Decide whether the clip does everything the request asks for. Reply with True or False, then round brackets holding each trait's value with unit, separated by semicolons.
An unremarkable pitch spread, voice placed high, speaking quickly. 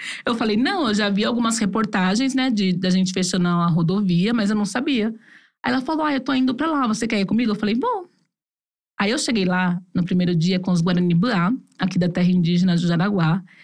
True (4.8 semitones; 205 Hz; 230 wpm)